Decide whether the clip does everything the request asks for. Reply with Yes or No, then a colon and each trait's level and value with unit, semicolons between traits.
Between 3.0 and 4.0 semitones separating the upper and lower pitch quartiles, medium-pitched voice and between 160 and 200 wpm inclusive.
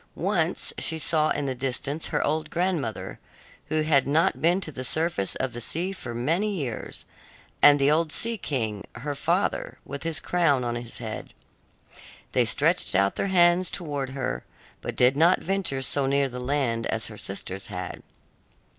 No: average, 4.9 semitones; medium, 145 Hz; average, 170 wpm